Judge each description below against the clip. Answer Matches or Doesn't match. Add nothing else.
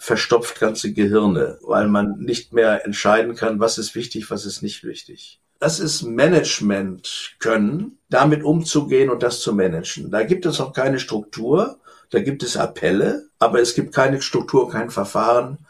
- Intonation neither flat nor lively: Doesn't match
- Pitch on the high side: Doesn't match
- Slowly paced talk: Doesn't match